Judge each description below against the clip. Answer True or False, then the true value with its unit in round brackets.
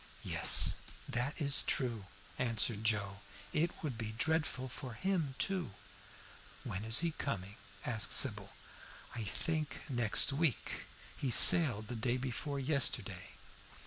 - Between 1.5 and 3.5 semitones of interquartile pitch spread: False (5.3 semitones)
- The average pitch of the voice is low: True (125 Hz)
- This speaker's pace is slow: True (125 wpm)